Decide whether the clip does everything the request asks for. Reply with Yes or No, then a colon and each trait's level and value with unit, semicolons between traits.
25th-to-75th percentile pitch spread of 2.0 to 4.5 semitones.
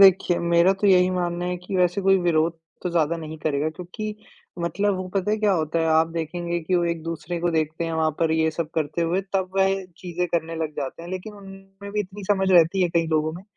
Yes: average, 2.7 semitones